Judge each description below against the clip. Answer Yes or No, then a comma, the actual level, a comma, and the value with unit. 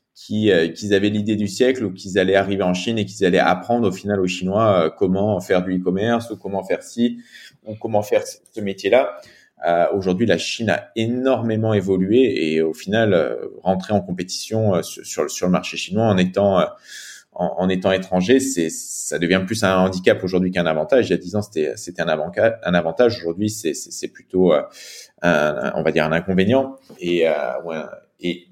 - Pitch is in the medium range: No, very low, 95 Hz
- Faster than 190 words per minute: Yes, average, 215 wpm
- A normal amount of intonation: Yes, average, 3.1 semitones